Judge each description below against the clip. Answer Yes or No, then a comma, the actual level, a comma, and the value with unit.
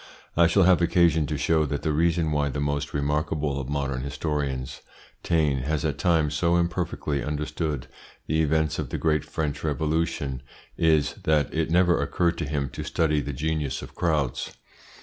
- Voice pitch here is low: Yes, very low, 75 Hz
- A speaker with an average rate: Yes, average, 170 wpm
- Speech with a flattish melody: Yes, narrow, 2.2 semitones